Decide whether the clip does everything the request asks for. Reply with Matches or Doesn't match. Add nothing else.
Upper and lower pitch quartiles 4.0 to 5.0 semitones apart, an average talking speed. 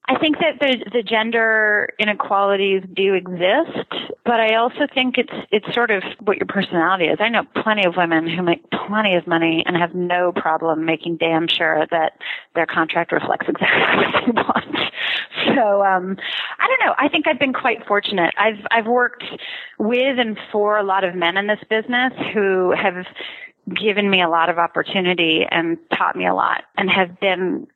Matches